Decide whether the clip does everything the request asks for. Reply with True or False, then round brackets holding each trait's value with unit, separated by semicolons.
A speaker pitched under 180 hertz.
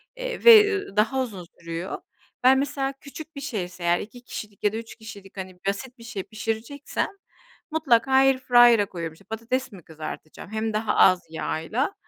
False (225 Hz)